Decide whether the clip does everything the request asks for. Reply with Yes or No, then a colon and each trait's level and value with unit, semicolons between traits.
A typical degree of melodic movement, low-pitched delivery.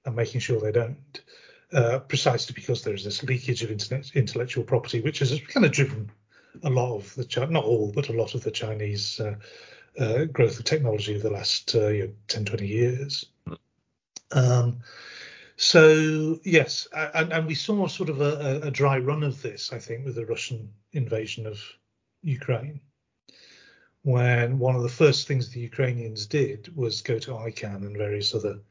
Yes: average, 4.3 semitones; low, 125 Hz